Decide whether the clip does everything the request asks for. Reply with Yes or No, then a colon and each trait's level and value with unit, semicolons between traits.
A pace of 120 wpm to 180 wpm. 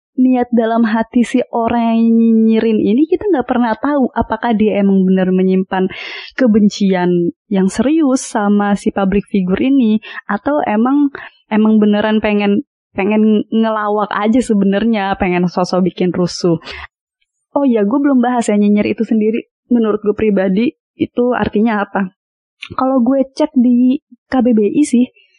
Yes: average, 135 wpm